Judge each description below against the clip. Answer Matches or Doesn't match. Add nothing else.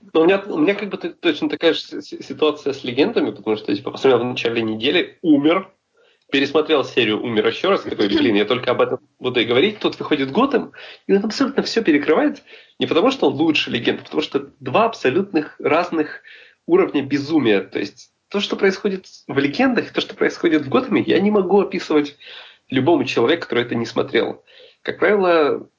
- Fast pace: Matches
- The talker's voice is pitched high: Matches